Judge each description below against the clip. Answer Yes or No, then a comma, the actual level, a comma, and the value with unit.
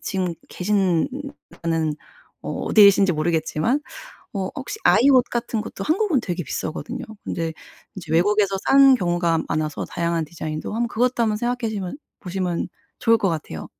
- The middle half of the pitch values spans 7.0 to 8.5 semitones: No, wide, 5.4 semitones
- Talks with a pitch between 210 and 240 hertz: No, high, 190 Hz